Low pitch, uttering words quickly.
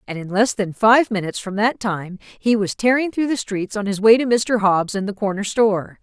No: high, 210 Hz; fast, 250 wpm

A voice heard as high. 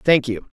No: low, 130 Hz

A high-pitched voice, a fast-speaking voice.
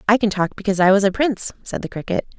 Yes: high, 205 Hz; fast, 275 wpm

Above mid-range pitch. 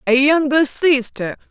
Yes: very high, 280 Hz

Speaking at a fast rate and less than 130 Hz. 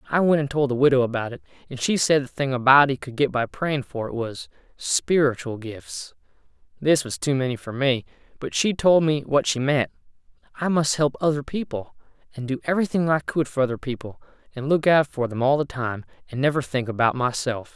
No: fast, 215 wpm; low, 135 Hz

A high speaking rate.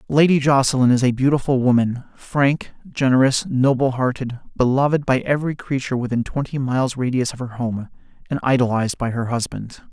No: average, 155 wpm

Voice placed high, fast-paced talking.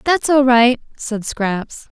No: high, 245 Hz; average, 150 wpm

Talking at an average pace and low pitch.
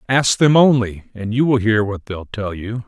No: fast, 230 wpm; low, 115 Hz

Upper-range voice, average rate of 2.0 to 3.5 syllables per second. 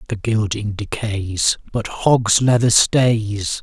No: low, 110 Hz; 3.1 syllables/s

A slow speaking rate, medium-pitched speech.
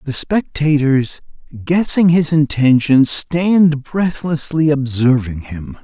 Yes: slow, 95 wpm; medium, 145 Hz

